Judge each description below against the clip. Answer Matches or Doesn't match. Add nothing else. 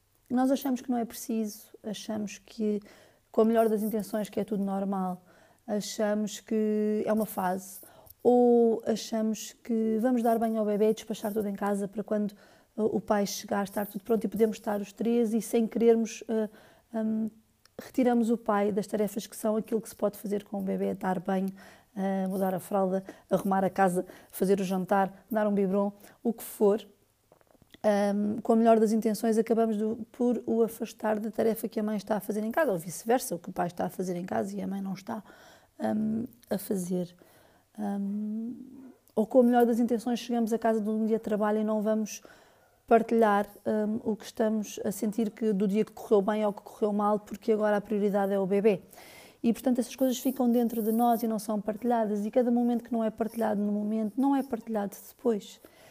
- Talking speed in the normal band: Doesn't match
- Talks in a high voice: Matches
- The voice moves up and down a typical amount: Doesn't match